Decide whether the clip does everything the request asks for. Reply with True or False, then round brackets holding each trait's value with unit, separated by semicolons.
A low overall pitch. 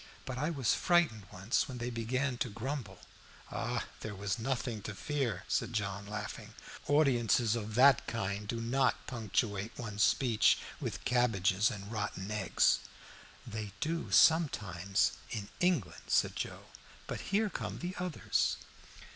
True (115 Hz)